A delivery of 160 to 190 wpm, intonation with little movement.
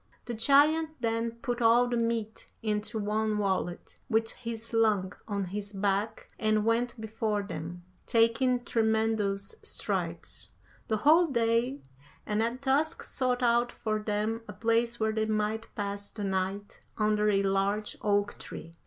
No: average, 145 wpm; narrow, 2.1 semitones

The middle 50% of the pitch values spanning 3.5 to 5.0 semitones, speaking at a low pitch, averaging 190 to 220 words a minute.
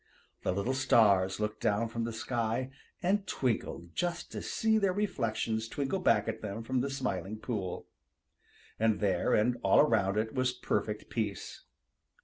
No: average, 3.8 semitones; low, 115 Hz; average, 155 wpm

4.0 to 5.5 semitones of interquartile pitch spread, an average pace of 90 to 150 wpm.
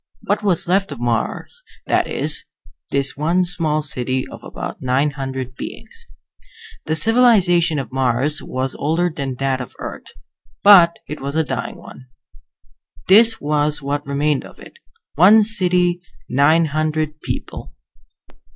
Yes: average, 4.4 semitones; average, 140 wpm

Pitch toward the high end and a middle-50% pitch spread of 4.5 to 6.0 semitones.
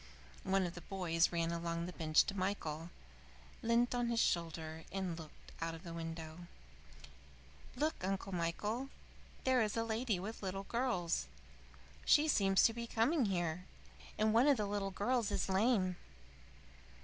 Yes: high, 195 Hz; average, 5.2 semitones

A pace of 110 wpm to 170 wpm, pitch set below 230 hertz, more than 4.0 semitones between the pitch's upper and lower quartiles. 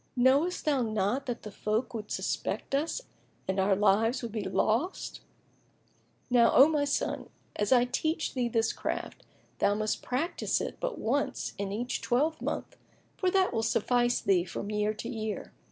No: average, 165 wpm; high, 240 Hz; average, 4.5 semitones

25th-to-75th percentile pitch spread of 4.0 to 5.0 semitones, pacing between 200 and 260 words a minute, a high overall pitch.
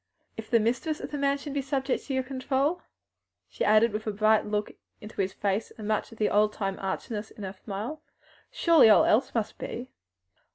Yes: average, 4.3 semitones; fast, 205 wpm; high, 220 Hz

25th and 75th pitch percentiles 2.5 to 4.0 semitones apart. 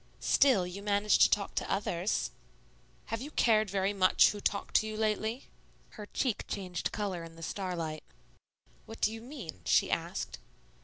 Yes: average, 2.9 semitones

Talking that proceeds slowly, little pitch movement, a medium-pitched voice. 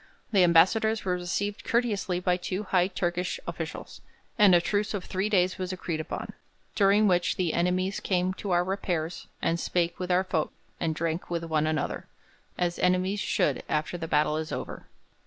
No: average, 175 wpm; narrow, 2.2 semitones; medium, 180 Hz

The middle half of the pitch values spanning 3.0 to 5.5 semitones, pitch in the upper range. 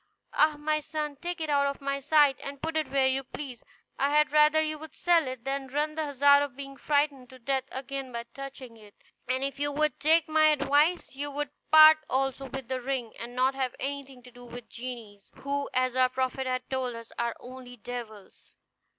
No: narrow, 2.5 semitones; very high, 275 Hz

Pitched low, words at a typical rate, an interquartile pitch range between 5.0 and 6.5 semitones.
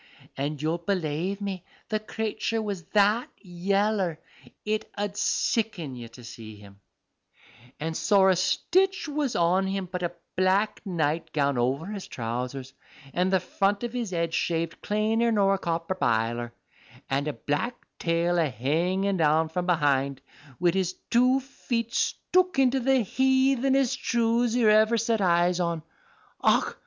No: medium, 185 Hz; average, 145 wpm; wide, 5.6 semitones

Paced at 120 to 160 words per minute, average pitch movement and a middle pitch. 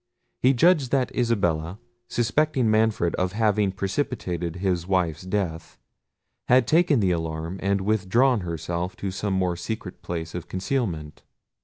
No: slow, 135 wpm; average, 4.9 semitones; very low, 95 Hz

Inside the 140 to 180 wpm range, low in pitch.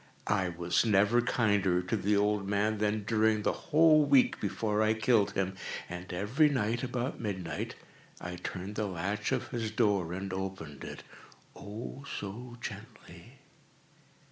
Yes: average, 145 wpm; low, 105 Hz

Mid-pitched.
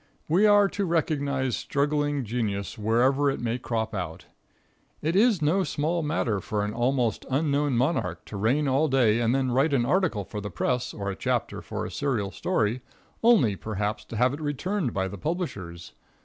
No: low, 130 Hz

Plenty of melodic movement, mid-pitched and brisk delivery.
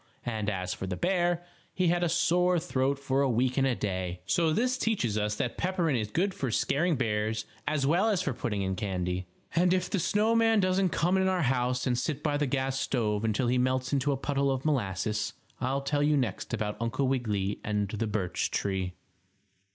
No: wide, 8.0 semitones; low, 130 Hz; fast, 210 wpm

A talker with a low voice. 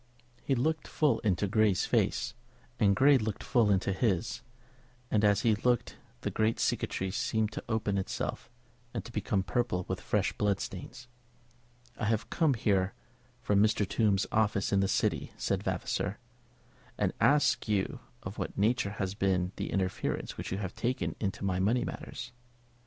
Yes: low, 105 Hz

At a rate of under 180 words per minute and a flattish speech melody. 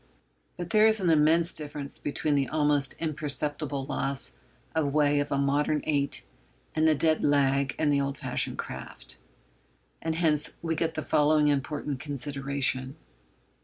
Yes: average, 150 wpm; narrow, 2.0 semitones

